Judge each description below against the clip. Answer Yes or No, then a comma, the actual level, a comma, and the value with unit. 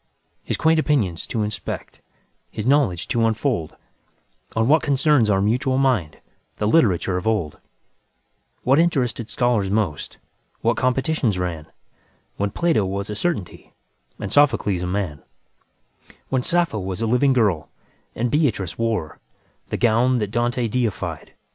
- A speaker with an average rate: No, slow, 110 wpm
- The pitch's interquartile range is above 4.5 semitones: Yes, average, 5.1 semitones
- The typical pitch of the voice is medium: No, low, 115 Hz